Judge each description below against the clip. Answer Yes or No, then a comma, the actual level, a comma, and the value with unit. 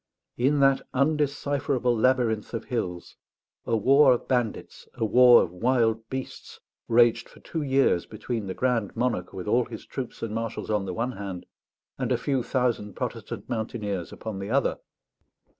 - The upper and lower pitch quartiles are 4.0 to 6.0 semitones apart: No, average, 3.3 semitones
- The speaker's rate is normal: Yes, average, 160 wpm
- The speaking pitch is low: Yes, low, 120 Hz